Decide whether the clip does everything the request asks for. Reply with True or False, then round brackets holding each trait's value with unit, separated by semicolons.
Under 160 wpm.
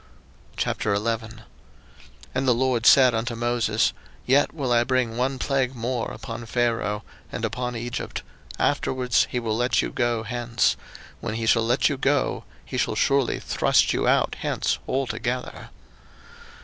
True (145 wpm)